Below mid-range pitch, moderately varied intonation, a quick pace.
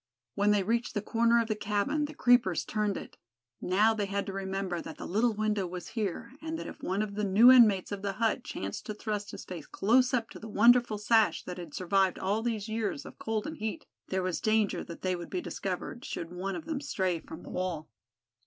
No: high, 210 Hz; average, 3.3 semitones; fast, 230 wpm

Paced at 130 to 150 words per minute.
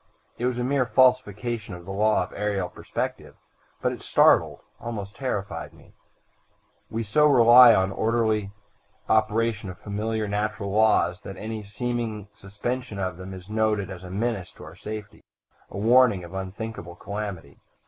No: average, 160 wpm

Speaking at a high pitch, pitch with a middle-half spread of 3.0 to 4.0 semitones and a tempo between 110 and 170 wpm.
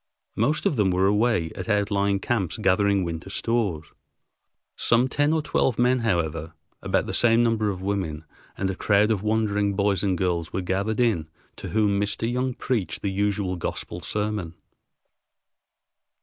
No: low, 100 Hz; average, 3.3 semitones; average, 160 wpm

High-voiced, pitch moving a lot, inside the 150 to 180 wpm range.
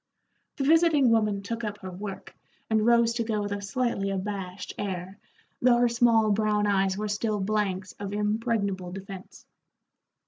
No: high, 210 Hz; average, 2.8 semitones; average, 160 wpm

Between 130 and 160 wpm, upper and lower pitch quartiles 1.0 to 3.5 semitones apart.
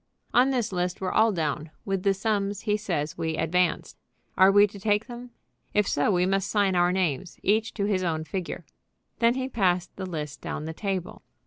No: average, 200 wpm; average, 3.0 semitones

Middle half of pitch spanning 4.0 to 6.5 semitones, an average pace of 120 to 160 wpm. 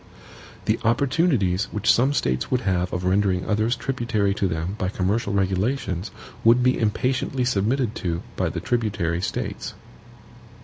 Yes: average, 4.9 semitones; average, 140 wpm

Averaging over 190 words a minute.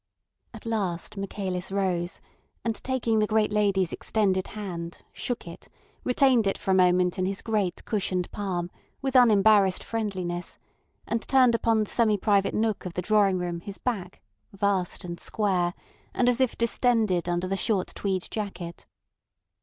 No: average, 155 wpm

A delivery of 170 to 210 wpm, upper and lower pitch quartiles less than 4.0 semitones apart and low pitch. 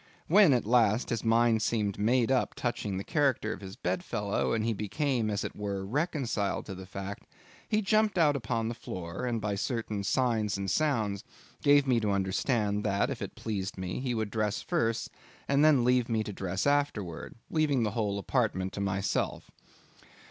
No: average, 185 wpm; average, 4.3 semitones; low, 110 Hz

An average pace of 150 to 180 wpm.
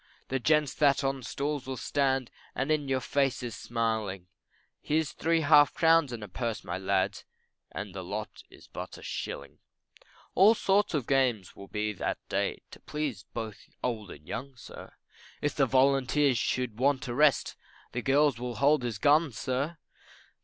Yes: average, 170 wpm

